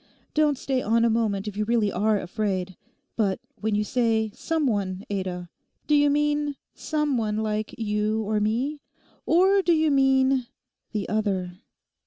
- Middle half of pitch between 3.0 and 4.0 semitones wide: No, average, 5.0 semitones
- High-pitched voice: Yes, high, 220 Hz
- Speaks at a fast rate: No, average, 150 wpm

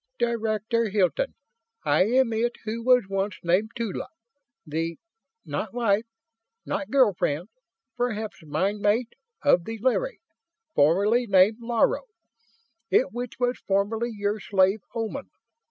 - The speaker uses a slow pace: Yes, slow, 120 wpm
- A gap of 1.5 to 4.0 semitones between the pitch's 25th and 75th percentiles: Yes, average, 3.4 semitones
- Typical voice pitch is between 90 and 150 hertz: No, high, 220 Hz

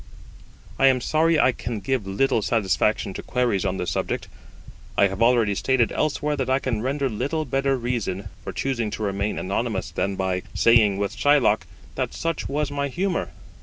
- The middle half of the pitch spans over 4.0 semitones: Yes, average, 5.2 semitones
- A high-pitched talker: No, low, 120 Hz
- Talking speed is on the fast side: No, average, 175 wpm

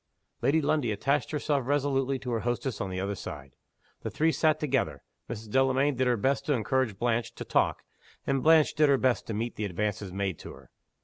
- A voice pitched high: No, low, 125 Hz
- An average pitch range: Yes, average, 4.9 semitones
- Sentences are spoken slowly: No, fast, 205 wpm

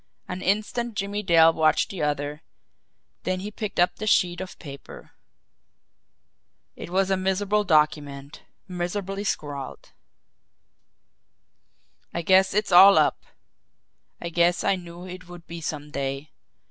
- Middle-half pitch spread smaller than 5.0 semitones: Yes, average, 3.9 semitones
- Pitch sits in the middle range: Yes, medium, 180 Hz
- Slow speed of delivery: Yes, slow, 130 wpm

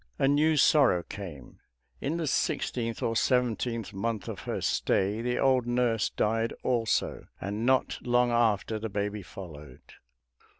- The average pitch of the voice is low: Yes, low, 115 Hz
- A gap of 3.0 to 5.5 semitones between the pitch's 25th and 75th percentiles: Yes, average, 3.3 semitones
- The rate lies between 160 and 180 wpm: No, average, 140 wpm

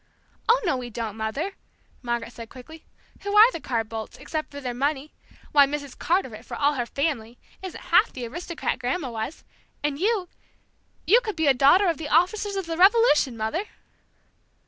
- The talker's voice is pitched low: No, very high, 290 Hz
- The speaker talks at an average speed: Yes, average, 180 wpm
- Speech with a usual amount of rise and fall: No, wide, 6.6 semitones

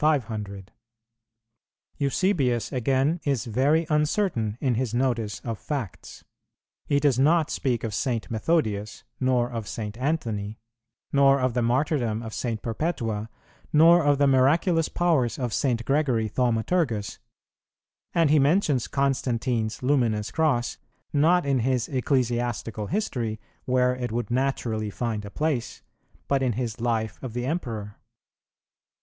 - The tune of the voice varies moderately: Yes, average, 4.1 semitones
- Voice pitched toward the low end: Yes, low, 125 Hz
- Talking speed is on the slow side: Yes, slow, 130 wpm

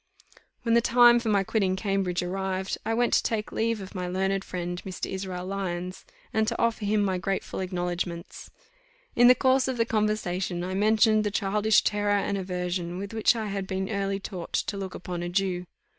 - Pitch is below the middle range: No, high, 195 Hz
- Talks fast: No, average, 195 wpm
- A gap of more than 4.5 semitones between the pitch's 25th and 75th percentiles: No, average, 2.8 semitones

